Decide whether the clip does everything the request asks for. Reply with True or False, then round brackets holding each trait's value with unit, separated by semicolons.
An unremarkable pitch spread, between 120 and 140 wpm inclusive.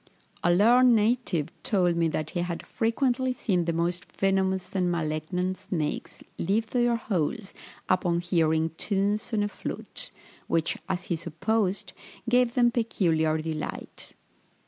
True (4.8 semitones; 135 wpm)